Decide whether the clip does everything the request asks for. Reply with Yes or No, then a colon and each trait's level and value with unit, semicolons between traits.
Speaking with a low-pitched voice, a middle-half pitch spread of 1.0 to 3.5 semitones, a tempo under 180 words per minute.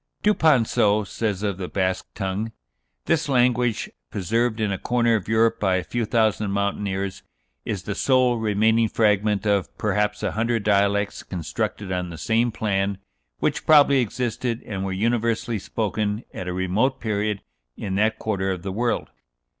Yes: low, 105 Hz; average, 2.9 semitones; average, 155 wpm